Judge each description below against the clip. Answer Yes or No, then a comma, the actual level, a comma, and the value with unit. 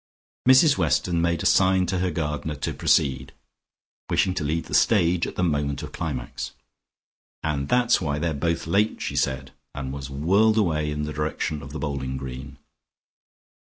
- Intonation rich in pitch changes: No, average, 4.3 semitones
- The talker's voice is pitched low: Yes, very low, 75 Hz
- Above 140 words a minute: Yes, average, 170 wpm